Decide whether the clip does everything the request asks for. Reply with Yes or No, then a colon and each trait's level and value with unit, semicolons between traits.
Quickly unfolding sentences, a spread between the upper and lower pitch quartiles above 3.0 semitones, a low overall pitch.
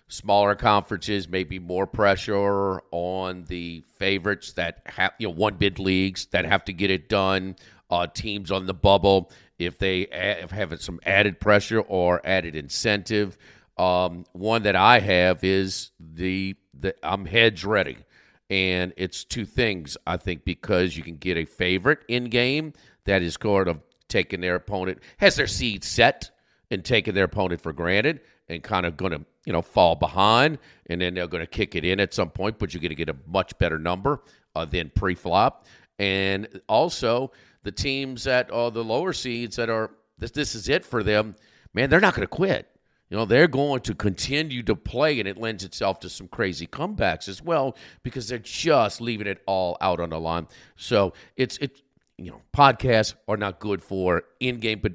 No: average, 190 wpm; average, 3.5 semitones; low, 100 Hz